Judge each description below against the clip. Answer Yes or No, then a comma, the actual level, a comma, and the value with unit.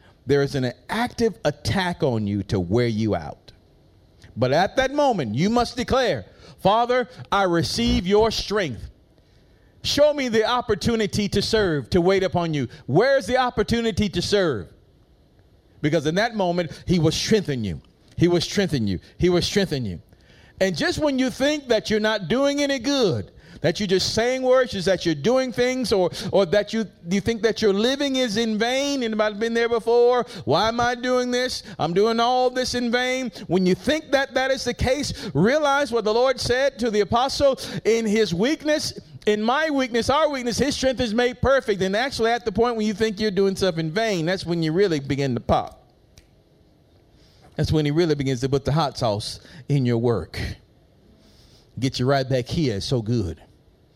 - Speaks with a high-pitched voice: Yes, high, 215 Hz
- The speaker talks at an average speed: Yes, average, 190 wpm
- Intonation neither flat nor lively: No, wide, 7.5 semitones